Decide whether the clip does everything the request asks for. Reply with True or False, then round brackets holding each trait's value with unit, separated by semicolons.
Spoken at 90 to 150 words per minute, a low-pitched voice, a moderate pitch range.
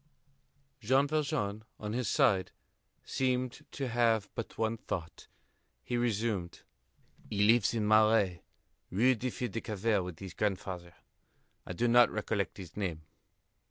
True (140 wpm; 110 Hz; 3.7 semitones)